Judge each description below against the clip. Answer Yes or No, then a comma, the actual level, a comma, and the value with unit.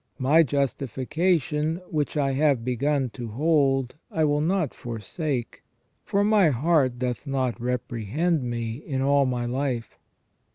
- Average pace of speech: No, slow, 130 wpm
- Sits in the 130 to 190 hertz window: Yes, low, 135 Hz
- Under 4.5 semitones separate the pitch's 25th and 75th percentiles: Yes, average, 3.8 semitones